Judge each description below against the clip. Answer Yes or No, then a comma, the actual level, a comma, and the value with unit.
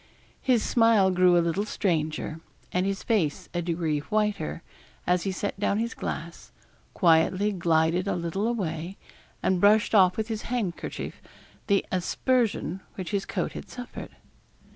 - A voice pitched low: No, high, 190 Hz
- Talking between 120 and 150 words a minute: Yes, average, 145 wpm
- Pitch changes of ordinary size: Yes, average, 3.8 semitones